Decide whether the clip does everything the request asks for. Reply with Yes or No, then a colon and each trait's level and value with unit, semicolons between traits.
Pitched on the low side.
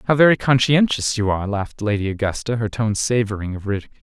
Yes: low, 110 Hz